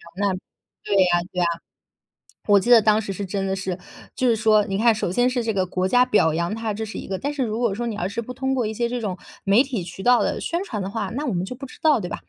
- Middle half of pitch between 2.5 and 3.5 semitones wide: No, average, 4.0 semitones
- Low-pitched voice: No, high, 215 Hz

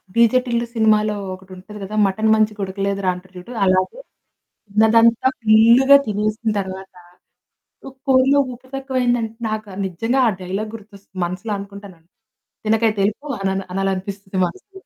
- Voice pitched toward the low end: No, high, 215 Hz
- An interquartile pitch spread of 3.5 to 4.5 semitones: No, average, 3.0 semitones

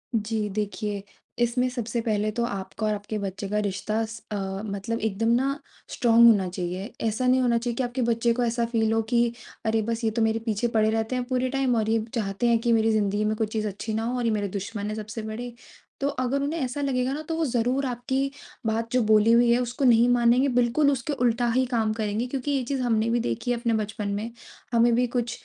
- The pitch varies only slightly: Yes, narrow, 2.3 semitones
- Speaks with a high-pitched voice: Yes, high, 230 Hz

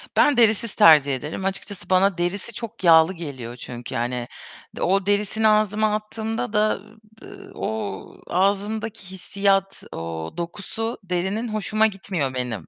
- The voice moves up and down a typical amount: No, wide, 6.0 semitones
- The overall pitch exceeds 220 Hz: No, high, 195 Hz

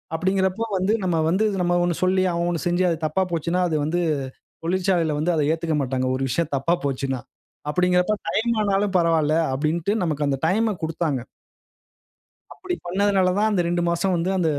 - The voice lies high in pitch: No, medium, 175 Hz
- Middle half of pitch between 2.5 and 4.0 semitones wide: Yes, average, 3.0 semitones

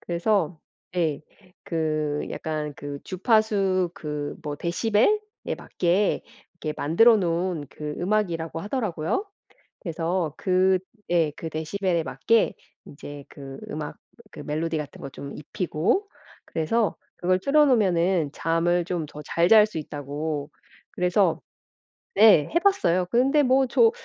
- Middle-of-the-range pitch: Yes, medium, 170 Hz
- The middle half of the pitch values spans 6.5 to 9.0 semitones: No, average, 5.2 semitones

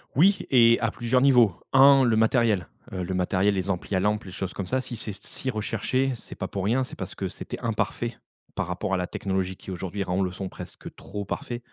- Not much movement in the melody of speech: No, average, 4.3 semitones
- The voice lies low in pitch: Yes, low, 105 Hz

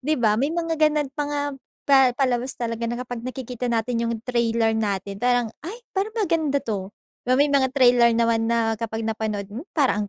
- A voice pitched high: Yes, high, 240 Hz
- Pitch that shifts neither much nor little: Yes, average, 3.8 semitones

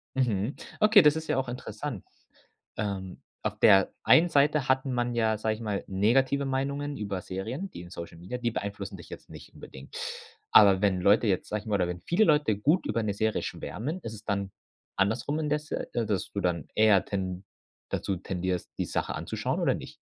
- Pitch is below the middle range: Yes, low, 110 Hz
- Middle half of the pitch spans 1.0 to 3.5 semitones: No, wide, 5.7 semitones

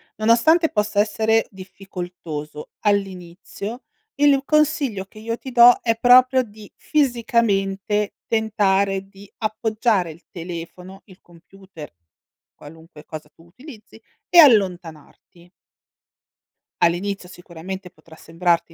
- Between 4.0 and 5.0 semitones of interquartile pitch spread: Yes, average, 4.3 semitones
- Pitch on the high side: Yes, high, 195 Hz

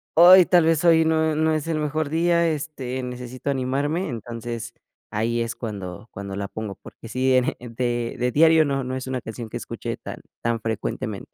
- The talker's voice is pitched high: No, low, 130 Hz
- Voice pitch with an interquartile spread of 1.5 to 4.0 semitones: No, average, 5.2 semitones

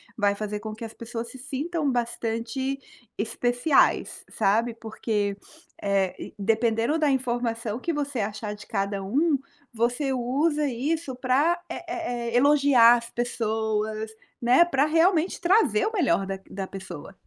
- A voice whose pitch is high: Yes, high, 240 Hz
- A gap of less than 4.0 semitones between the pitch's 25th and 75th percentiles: No, average, 4.7 semitones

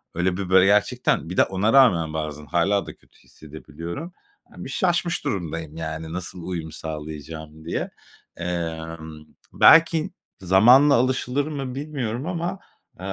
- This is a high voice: No, very low, 90 Hz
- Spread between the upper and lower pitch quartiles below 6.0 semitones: No, wide, 8.4 semitones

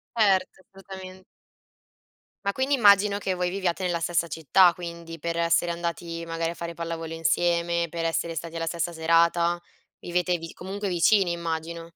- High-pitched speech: No, medium, 170 Hz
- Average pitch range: No, narrow, 1.8 semitones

